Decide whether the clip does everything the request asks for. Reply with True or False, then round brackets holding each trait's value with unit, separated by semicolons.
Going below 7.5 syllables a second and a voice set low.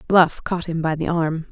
False (4.6 syllables/s; 165 Hz)